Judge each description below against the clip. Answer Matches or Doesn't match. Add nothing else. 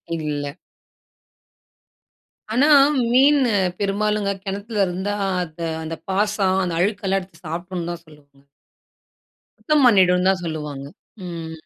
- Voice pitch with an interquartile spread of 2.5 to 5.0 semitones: Matches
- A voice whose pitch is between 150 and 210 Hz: Matches